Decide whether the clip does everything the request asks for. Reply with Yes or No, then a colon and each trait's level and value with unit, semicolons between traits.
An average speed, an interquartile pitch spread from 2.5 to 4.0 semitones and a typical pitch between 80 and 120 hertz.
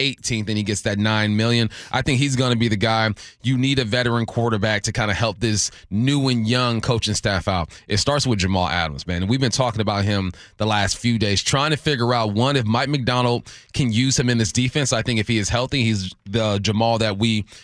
No: fast, 240 wpm; average, 2.8 semitones; low, 115 Hz